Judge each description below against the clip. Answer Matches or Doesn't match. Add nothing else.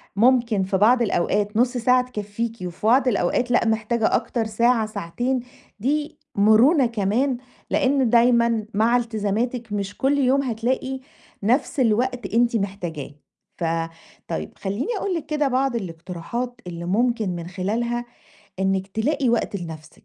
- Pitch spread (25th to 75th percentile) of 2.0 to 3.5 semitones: Doesn't match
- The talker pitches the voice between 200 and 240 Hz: Matches